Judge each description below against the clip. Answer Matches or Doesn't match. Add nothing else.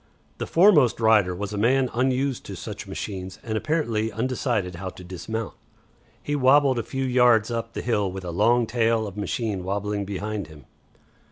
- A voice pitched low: Matches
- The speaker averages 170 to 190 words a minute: Matches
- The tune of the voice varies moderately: Matches